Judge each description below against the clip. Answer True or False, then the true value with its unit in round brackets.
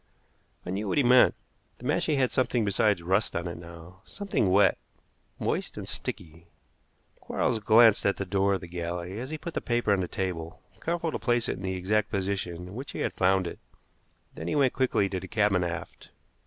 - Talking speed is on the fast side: True (210 wpm)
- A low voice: True (100 Hz)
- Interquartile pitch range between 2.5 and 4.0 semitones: False (5.0 semitones)